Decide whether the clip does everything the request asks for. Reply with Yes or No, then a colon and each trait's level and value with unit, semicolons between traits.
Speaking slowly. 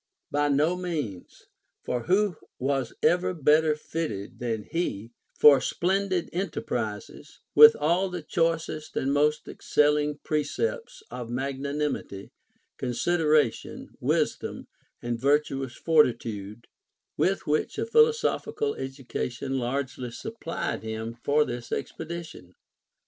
Yes: slow, 105 wpm